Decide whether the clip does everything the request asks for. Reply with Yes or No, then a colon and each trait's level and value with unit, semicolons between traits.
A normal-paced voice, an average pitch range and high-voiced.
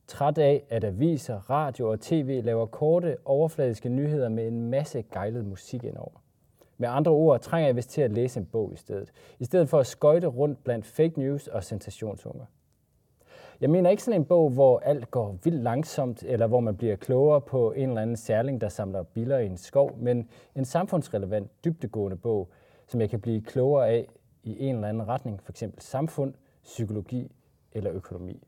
No: average, 190 wpm; average, 4.2 semitones; low, 125 Hz